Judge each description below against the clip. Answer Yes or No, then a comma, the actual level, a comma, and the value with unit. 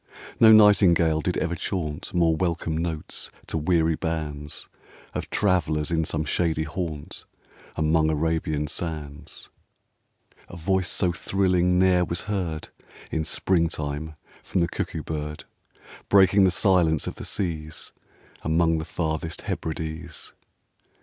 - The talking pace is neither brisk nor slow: No, slow, 125 wpm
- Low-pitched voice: Yes, very low, 80 Hz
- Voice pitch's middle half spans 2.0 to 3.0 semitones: Yes, narrow, 2.4 semitones